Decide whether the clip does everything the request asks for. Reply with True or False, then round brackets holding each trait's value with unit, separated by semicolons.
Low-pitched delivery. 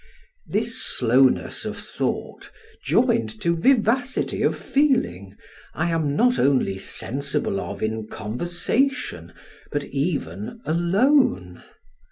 False (145 Hz)